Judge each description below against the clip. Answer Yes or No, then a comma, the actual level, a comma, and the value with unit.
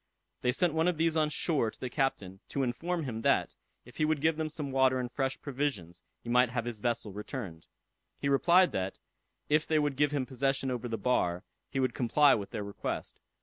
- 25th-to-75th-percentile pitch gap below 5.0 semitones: Yes, average, 4.3 semitones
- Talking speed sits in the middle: No, fast, 215 wpm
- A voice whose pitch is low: Yes, low, 130 Hz